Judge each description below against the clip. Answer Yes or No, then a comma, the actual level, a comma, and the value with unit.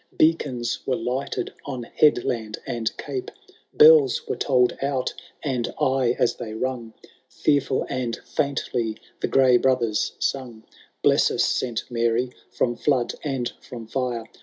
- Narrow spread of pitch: Yes, narrow, 2.2 semitones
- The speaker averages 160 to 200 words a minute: No, slow, 135 wpm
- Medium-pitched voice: No, low, 125 Hz